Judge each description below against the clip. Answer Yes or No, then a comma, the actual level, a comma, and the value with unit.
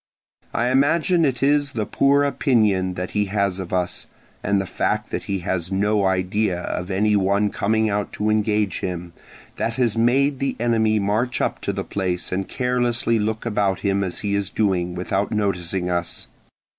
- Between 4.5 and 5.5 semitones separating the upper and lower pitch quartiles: No, average, 3.6 semitones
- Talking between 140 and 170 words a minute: No, average, 180 wpm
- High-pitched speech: No, low, 105 Hz